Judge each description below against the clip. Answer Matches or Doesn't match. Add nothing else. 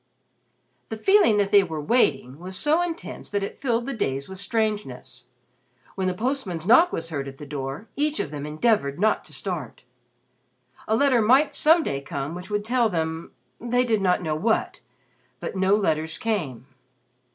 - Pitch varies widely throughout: Matches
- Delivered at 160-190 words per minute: Matches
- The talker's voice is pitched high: Matches